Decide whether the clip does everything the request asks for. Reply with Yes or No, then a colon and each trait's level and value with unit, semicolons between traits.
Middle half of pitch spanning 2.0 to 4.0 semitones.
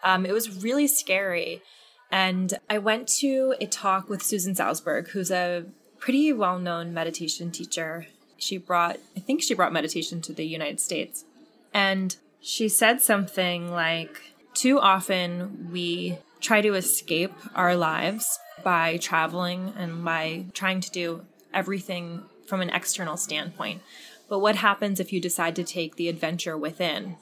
Yes: average, 3.1 semitones